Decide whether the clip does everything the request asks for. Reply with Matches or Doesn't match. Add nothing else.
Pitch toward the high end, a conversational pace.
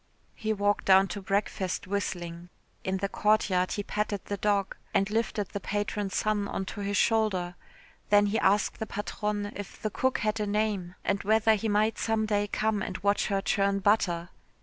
Matches